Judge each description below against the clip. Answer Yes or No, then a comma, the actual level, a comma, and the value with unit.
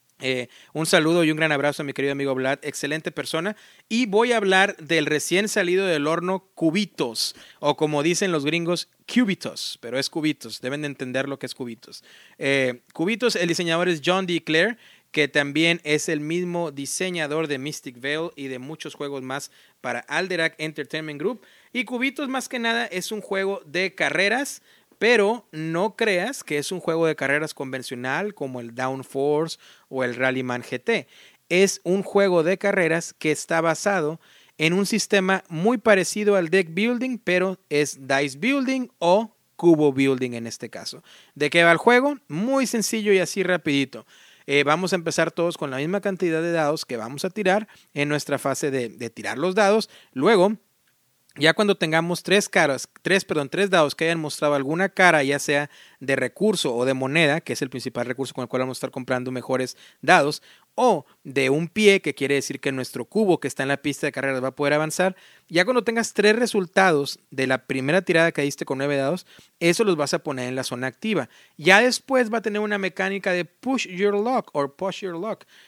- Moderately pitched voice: Yes, medium, 165 Hz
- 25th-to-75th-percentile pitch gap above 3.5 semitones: Yes, wide, 5.5 semitones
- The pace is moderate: No, fast, 195 wpm